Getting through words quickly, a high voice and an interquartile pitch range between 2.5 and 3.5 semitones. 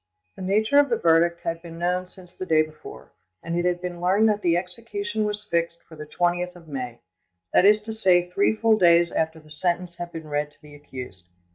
No: fast, 220 wpm; medium, 175 Hz; average, 3.2 semitones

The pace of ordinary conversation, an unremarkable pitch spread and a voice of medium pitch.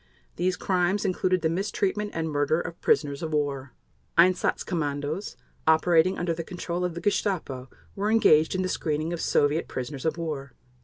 Yes: average, 165 wpm; average, 3.7 semitones; medium, 165 Hz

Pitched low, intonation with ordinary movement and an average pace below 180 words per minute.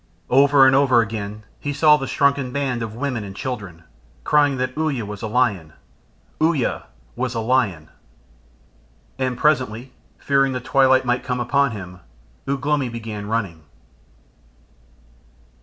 Yes: low, 125 Hz; average, 4.0 semitones; average, 140 wpm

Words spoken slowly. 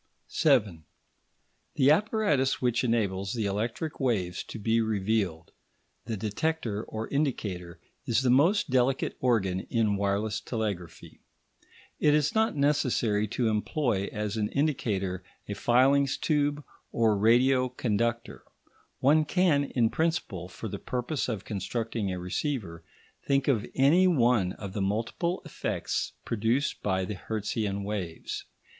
Yes: slow, 130 wpm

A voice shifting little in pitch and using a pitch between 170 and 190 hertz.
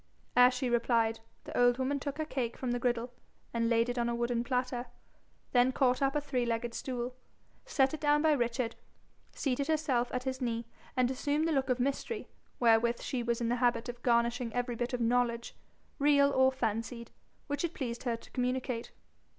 No: narrow, 2.0 semitones; high, 245 Hz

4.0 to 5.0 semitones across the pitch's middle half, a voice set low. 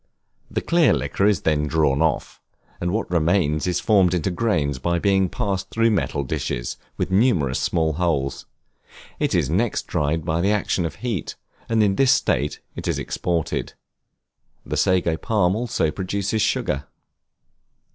Yes: average, 4.6 semitones; very low, 90 Hz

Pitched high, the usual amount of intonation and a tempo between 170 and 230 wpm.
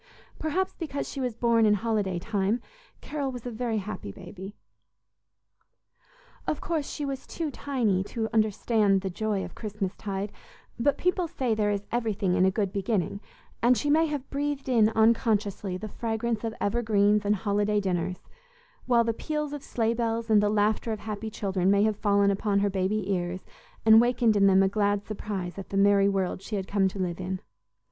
Yes: high, 210 Hz; average, 3.0 semitones; average, 185 wpm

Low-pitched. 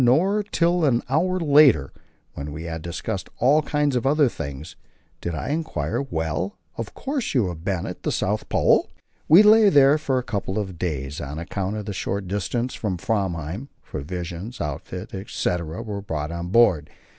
Yes: low, 100 Hz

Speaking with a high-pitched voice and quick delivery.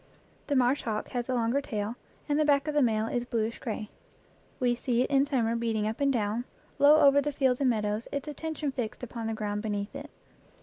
Yes: high, 245 Hz; fast, 220 wpm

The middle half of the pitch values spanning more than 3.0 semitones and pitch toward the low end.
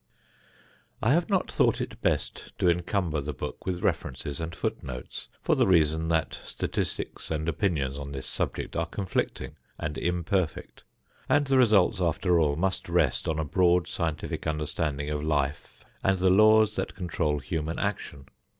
Yes: average, 3.8 semitones; very low, 85 Hz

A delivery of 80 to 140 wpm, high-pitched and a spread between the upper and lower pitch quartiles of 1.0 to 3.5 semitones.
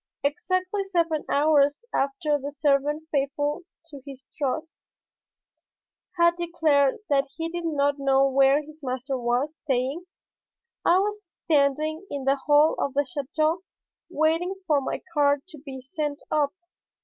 Yes: slow, 135 wpm; very high, 290 Hz; average, 2.7 semitones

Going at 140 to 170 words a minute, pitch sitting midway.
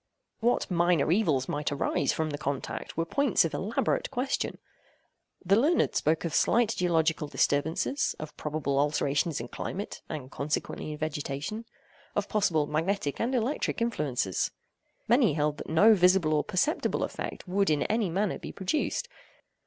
Yes: average, 150 wpm; medium, 165 Hz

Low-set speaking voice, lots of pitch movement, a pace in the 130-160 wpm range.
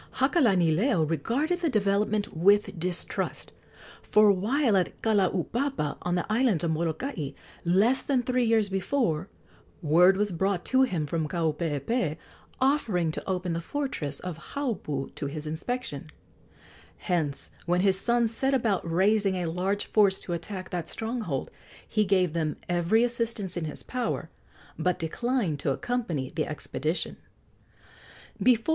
No: high, 190 Hz; wide, 5.9 semitones; slow, 135 wpm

